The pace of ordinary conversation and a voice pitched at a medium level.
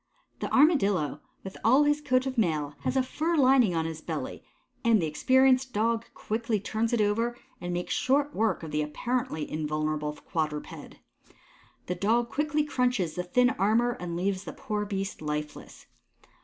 No: average, 165 wpm; high, 215 Hz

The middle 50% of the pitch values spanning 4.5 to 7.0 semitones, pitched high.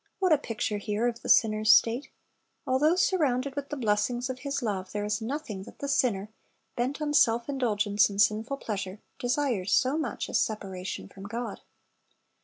Yes: average, 4.9 semitones; high, 235 Hz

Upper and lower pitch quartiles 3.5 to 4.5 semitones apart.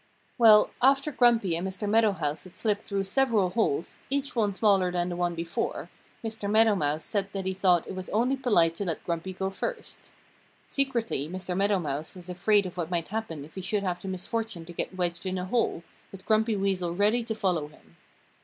Yes: average, 3.9 semitones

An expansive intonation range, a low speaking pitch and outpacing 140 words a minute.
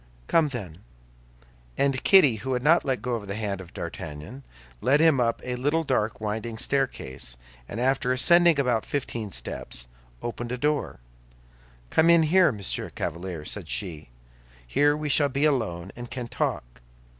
Yes: wide, 5.8 semitones; low, 125 Hz; average, 155 wpm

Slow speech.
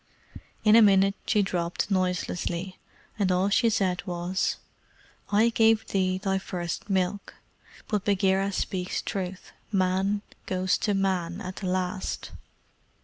Yes: slow, 130 wpm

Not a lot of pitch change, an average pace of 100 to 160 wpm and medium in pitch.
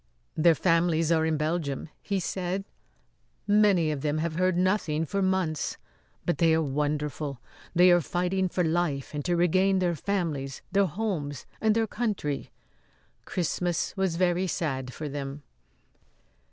No: average, 3.6 semitones; average, 145 wpm; medium, 170 Hz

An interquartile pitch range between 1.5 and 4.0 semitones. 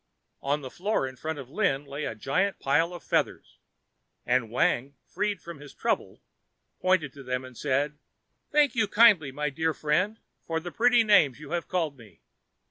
No: average, 5.2 semitones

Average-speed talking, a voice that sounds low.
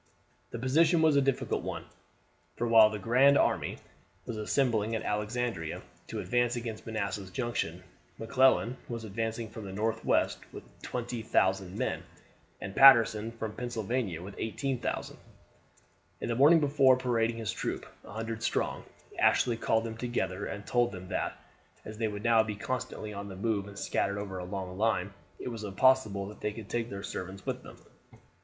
Yes: average, 165 wpm; low, 110 Hz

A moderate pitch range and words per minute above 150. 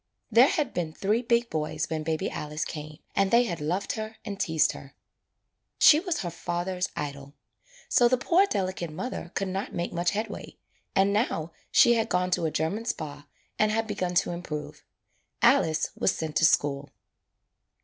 No: wide, 5.7 semitones; average, 175 wpm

